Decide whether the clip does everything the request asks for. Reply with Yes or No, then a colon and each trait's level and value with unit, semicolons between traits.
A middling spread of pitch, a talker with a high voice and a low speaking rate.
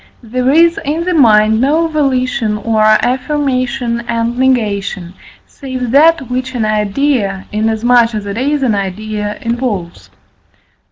Yes: average, 3.8 semitones; high, 240 Hz; slow, 125 wpm